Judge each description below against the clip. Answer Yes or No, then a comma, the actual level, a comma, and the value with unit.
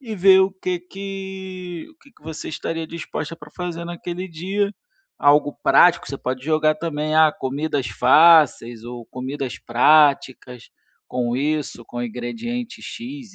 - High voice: No, medium, 160 Hz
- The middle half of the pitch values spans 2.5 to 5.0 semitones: No, wide, 5.5 semitones